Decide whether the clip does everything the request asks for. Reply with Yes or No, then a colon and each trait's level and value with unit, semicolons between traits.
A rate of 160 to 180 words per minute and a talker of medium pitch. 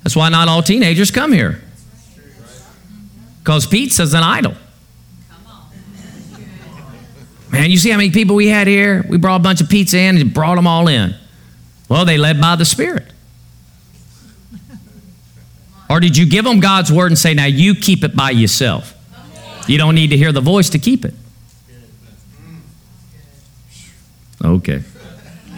No: average, 150 wpm; medium, 155 Hz